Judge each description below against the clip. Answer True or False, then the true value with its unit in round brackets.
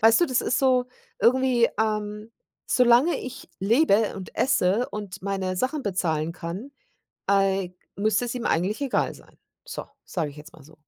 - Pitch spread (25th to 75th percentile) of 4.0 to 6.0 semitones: True (5.1 semitones)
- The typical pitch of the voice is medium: False (210 Hz)